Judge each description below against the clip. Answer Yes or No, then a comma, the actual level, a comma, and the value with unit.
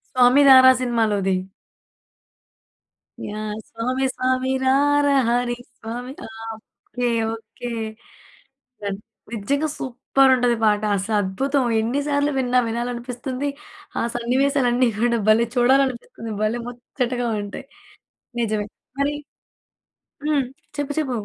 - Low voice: No, high, 245 Hz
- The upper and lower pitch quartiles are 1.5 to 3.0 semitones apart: Yes, narrow, 2.6 semitones